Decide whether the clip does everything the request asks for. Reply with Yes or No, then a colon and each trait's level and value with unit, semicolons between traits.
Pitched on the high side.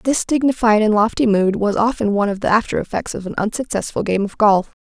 Yes: high, 215 Hz